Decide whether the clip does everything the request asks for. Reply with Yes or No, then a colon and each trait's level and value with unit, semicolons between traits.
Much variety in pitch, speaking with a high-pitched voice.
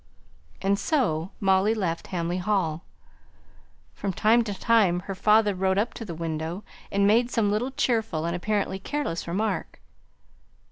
No: average, 3.8 semitones; high, 200 Hz